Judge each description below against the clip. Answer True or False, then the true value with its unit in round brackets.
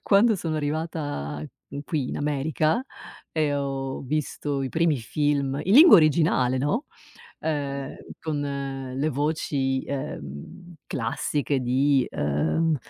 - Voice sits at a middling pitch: True (145 Hz)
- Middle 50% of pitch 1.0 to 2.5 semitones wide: False (2.9 semitones)